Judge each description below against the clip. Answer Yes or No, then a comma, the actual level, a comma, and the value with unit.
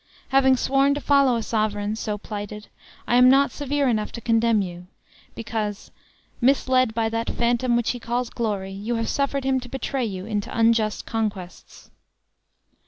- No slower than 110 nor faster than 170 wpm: Yes, average, 165 wpm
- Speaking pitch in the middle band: No, high, 230 Hz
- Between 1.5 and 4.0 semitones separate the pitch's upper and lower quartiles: Yes, average, 3.3 semitones